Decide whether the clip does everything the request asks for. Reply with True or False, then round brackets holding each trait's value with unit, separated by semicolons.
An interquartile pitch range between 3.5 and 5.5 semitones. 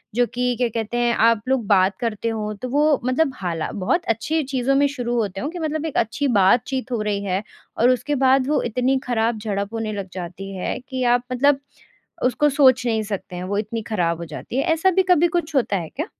True (4.7 semitones)